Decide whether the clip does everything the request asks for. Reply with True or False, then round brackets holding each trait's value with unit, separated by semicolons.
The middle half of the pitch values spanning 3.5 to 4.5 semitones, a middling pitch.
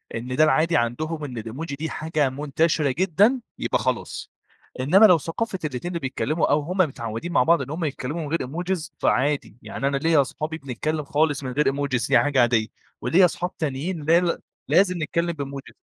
True (3.8 semitones; 150 Hz)